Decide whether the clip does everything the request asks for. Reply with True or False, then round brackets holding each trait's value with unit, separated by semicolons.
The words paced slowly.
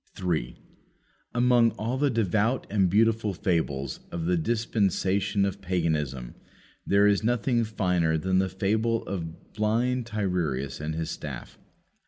True (130 wpm)